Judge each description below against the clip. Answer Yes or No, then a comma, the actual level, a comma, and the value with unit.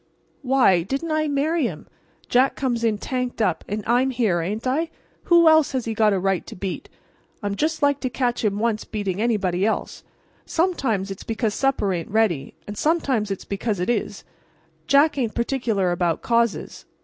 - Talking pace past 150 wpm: Yes, average, 180 wpm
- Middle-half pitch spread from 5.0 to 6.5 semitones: Yes, average, 5.3 semitones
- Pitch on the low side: No, high, 230 Hz